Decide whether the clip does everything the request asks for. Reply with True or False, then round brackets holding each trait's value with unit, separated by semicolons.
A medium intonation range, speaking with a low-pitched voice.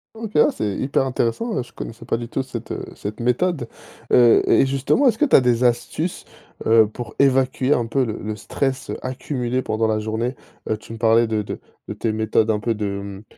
True (3.2 semitones; 120 Hz)